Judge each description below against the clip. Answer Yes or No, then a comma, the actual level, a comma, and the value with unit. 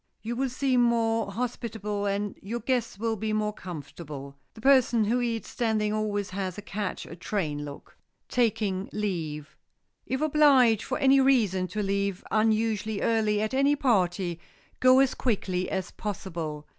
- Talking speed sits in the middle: Yes, average, 155 wpm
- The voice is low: No, high, 215 Hz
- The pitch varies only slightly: No, average, 3.9 semitones